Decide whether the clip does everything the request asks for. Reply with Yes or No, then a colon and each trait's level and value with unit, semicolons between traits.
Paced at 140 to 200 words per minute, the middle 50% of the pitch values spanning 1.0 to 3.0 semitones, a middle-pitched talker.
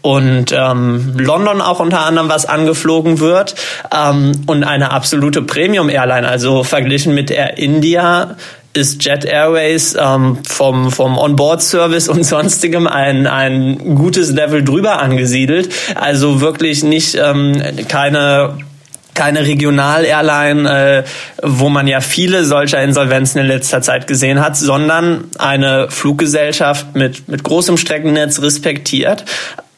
No: average, 130 wpm; narrow, 2.4 semitones; medium, 145 Hz